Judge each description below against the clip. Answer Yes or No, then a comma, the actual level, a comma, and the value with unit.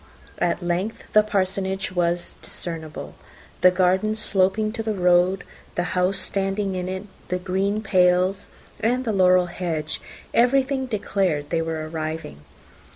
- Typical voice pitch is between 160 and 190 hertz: Yes, medium, 185 Hz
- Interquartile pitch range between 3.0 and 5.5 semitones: No, narrow, 2.6 semitones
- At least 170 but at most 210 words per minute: No, slow, 135 wpm